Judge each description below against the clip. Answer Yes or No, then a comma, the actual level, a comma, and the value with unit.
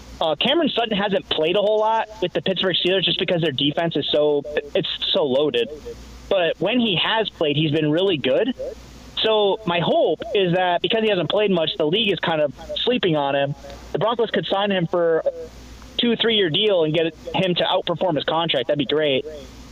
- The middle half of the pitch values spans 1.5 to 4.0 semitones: No, average, 5.1 semitones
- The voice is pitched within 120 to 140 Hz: No, medium, 185 Hz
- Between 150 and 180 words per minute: No, fast, 205 wpm